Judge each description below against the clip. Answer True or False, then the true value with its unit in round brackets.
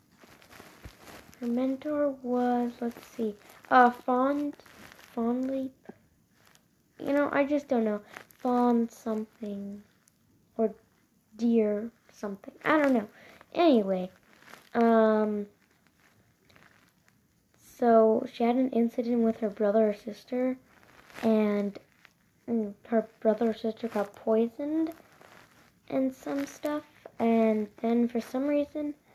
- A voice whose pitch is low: False (235 Hz)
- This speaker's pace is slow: True (100 wpm)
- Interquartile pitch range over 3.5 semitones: False (3.2 semitones)